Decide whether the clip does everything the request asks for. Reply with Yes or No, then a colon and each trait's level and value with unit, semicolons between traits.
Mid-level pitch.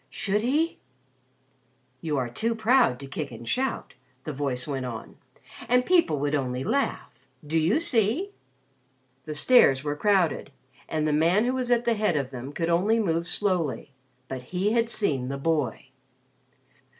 Yes: medium, 165 Hz